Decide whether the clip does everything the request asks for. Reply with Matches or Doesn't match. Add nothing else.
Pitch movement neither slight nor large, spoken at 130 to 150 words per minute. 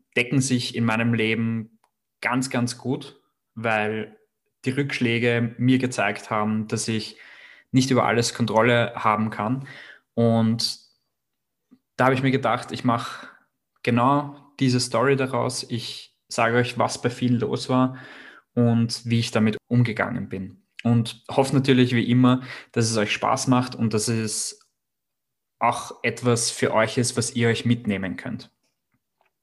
Doesn't match